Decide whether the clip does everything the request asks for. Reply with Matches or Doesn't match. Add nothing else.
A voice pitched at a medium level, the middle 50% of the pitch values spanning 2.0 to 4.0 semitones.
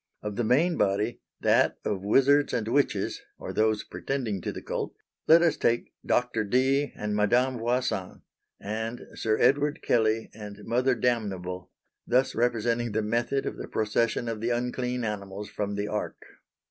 Doesn't match